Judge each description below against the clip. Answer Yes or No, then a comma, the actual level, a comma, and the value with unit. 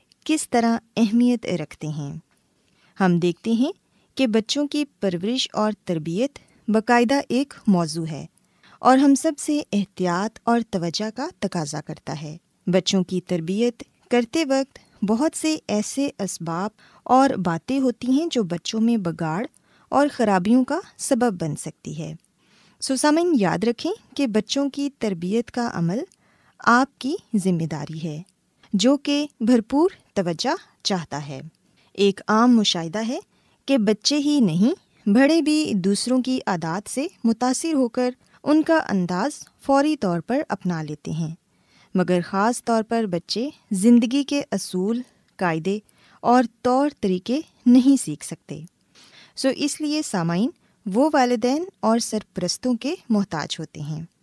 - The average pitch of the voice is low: No, high, 225 Hz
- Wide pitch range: Yes, wide, 6.6 semitones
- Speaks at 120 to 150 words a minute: Yes, average, 140 wpm